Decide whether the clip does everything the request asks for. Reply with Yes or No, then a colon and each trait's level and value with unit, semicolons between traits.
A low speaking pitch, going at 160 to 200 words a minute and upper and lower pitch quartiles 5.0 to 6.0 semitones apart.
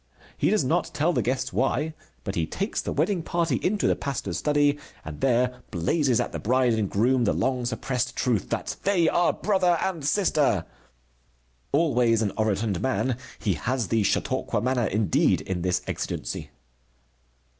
Yes: low, 125 Hz; average, 165 wpm; wide, 5.5 semitones